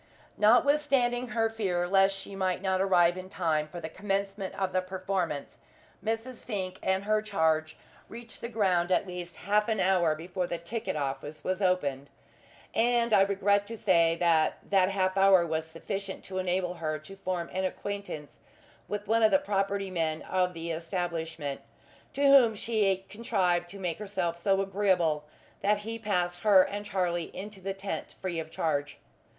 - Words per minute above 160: Yes, average, 170 wpm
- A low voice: No, high, 190 Hz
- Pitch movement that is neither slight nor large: Yes, average, 3.0 semitones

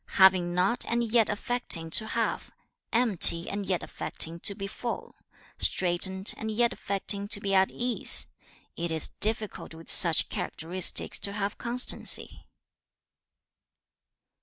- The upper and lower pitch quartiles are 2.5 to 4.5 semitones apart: Yes, average, 3.9 semitones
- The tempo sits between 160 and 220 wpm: No, slow, 135 wpm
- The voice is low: No, high, 200 Hz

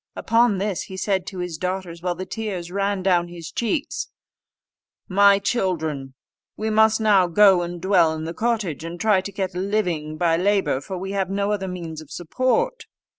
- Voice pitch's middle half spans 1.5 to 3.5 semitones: Yes, average, 3.0 semitones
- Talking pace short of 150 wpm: No, average, 185 wpm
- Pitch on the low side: No, high, 190 Hz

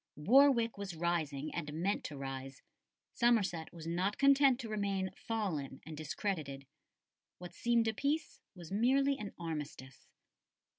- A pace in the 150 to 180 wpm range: No, slow, 135 wpm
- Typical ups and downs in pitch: No, wide, 6.8 semitones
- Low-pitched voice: No, medium, 185 Hz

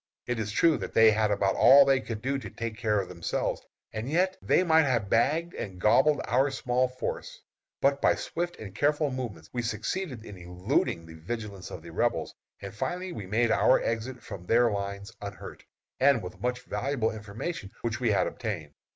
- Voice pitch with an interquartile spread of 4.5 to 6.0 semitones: Yes, average, 5.1 semitones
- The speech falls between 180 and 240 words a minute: Yes, average, 195 wpm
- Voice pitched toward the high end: No, low, 115 Hz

